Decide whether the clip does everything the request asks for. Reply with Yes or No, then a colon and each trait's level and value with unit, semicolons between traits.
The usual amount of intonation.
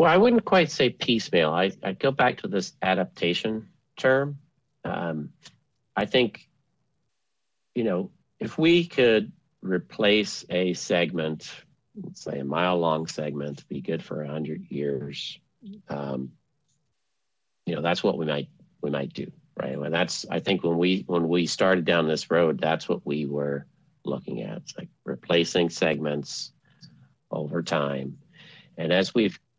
No: wide, 6.9 semitones